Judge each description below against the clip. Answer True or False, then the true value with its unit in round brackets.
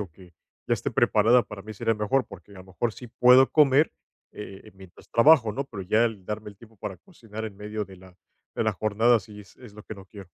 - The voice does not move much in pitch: False (3.2 semitones)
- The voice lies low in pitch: True (105 Hz)